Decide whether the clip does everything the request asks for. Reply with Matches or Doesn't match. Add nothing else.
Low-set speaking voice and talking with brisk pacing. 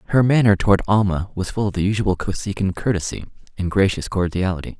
Doesn't match